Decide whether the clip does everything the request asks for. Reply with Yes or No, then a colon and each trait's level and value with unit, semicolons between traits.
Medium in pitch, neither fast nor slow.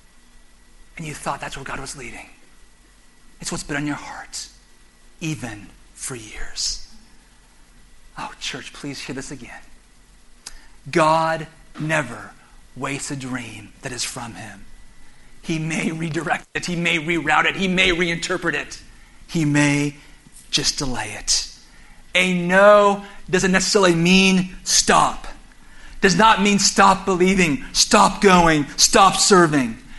No: medium, 155 Hz; slow, 130 wpm